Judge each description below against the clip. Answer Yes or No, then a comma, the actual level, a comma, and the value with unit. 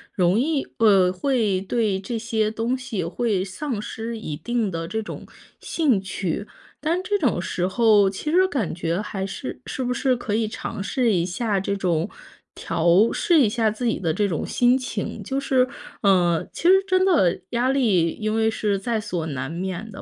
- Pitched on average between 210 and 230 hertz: Yes, high, 215 Hz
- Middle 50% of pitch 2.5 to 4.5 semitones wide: No, average, 4.9 semitones